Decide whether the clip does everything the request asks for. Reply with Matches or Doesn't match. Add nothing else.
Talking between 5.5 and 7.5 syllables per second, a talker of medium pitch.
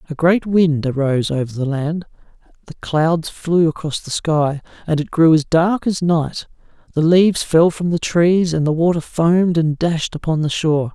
Doesn't match